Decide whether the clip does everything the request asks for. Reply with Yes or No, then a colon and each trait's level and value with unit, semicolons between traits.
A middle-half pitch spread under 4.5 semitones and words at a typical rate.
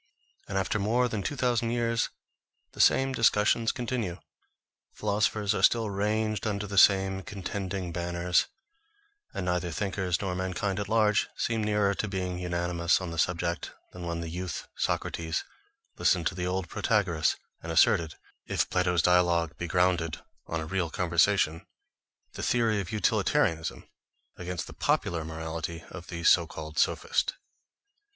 Yes: average, 3.5 semitones; average, 145 wpm